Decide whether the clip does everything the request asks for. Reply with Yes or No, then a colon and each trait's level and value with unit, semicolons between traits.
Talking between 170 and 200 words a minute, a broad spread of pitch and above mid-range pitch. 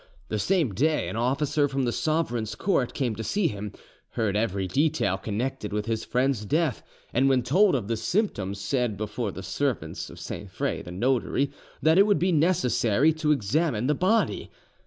No: average, 180 wpm; wide, 6.4 semitones; low, 125 Hz